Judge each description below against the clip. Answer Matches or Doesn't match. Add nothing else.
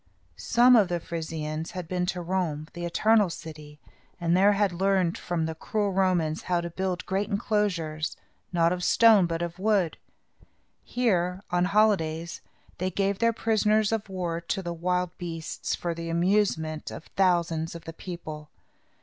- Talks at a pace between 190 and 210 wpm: Doesn't match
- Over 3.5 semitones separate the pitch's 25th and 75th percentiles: Doesn't match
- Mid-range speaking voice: Matches